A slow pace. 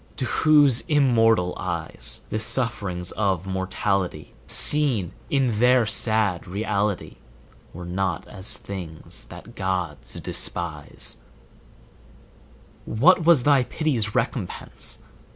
Yes: slow, 100 wpm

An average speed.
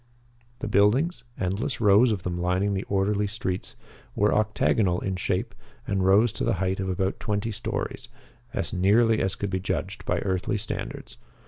Yes: average, 165 wpm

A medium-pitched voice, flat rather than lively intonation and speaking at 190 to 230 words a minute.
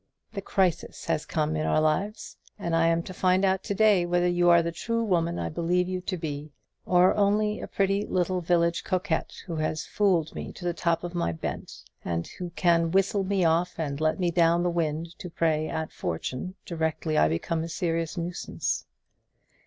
Yes: medium, 170 Hz; narrow, 2.3 semitones; average, 195 wpm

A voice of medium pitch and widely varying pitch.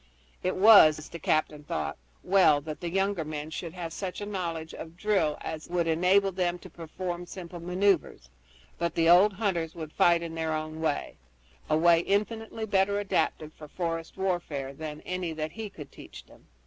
No: medium, 170 Hz; average, 3.3 semitones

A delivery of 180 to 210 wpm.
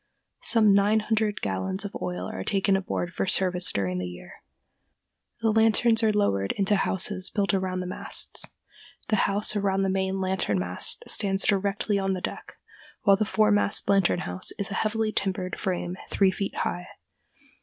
No: average, 165 wpm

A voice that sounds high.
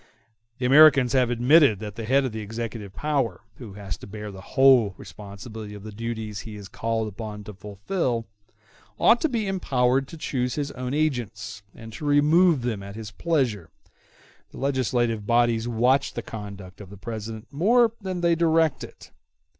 No: low, 120 Hz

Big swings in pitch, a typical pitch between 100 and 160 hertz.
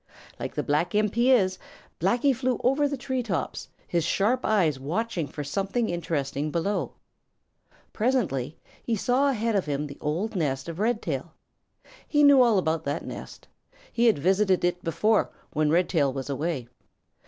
No: wide, 7.2 semitones; medium, 185 Hz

